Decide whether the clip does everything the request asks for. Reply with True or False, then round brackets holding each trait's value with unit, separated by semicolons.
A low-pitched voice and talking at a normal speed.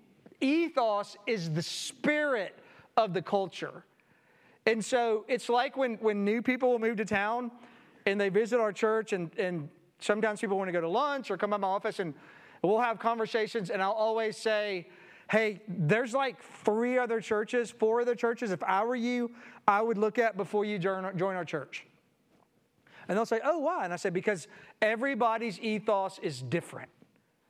False (215 Hz; 180 wpm)